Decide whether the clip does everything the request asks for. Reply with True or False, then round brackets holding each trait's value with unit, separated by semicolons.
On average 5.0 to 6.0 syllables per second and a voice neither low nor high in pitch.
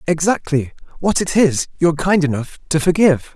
True (5.4 syllables/s; 160 Hz)